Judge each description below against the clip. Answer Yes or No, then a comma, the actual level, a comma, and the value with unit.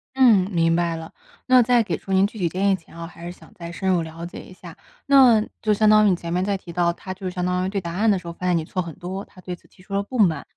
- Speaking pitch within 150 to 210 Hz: Yes, medium, 185 Hz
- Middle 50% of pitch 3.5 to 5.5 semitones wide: No, average, 2.8 semitones